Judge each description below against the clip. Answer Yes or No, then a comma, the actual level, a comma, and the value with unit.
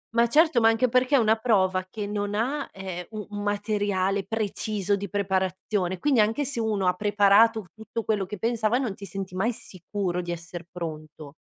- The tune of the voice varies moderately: Yes, average, 3.1 semitones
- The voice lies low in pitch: No, high, 205 Hz